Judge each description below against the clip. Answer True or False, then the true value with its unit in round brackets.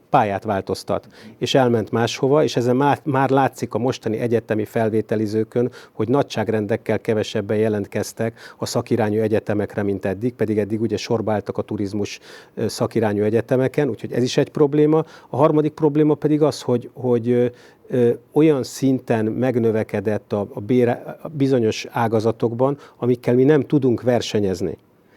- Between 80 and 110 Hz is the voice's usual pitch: False (120 Hz)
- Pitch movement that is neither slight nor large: True (3.3 semitones)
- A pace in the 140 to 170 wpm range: False (125 wpm)